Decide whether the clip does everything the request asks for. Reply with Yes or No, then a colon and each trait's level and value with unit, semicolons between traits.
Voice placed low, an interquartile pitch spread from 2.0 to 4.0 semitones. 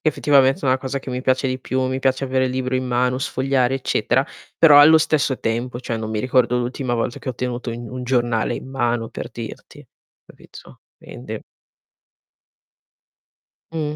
No: low, 130 Hz; narrow, 1.6 semitones